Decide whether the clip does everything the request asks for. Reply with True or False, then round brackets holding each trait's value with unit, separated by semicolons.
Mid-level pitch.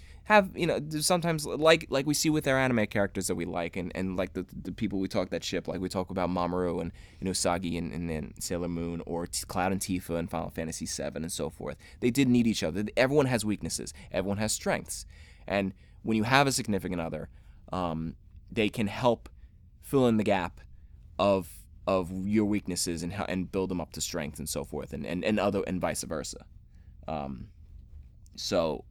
False (90 Hz)